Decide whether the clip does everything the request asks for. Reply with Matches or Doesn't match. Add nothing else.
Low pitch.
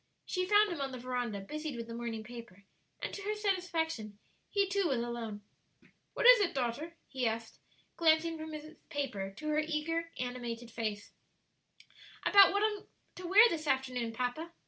Doesn't match